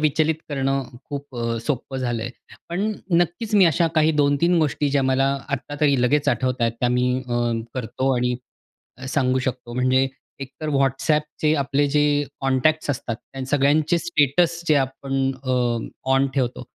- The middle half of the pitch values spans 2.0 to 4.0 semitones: Yes, average, 2.8 semitones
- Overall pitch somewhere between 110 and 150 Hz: Yes, low, 135 Hz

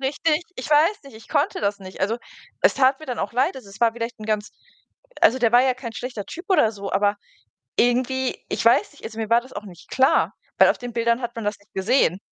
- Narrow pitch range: No, average, 3.6 semitones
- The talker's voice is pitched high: Yes, high, 235 Hz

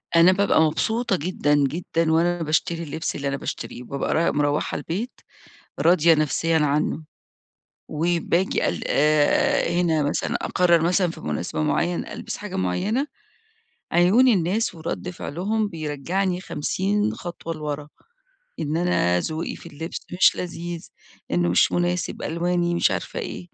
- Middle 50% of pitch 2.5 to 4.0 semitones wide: Yes, average, 2.9 semitones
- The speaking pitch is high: No, medium, 170 Hz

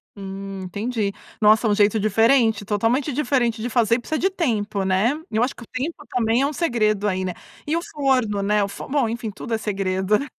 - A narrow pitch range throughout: No, average, 3.8 semitones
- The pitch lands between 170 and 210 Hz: No, high, 220 Hz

